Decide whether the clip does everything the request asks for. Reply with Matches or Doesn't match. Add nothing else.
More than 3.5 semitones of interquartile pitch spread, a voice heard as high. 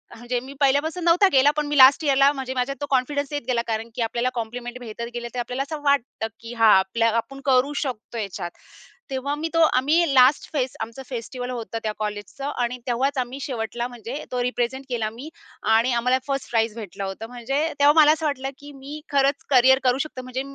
Doesn't match